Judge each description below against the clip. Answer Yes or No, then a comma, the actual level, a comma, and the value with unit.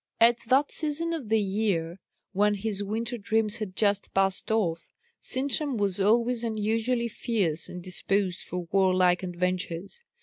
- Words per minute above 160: No, average, 140 wpm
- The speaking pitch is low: No, high, 205 Hz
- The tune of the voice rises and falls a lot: No, average, 3.9 semitones